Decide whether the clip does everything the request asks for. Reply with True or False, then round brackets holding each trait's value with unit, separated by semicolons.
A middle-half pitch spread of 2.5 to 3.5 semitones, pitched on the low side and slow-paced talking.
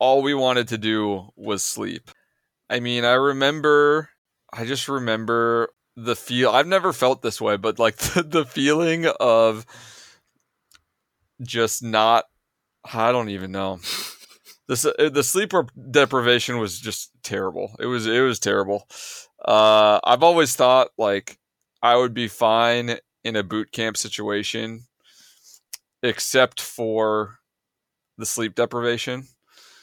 True (2.9 semitones; 120 Hz; 125 wpm)